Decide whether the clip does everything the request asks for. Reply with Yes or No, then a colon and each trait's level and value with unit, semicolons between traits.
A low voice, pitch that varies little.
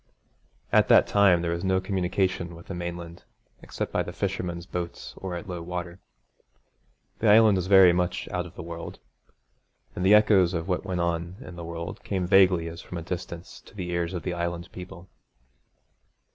Yes: very low, 90 Hz; narrow, 1.5 semitones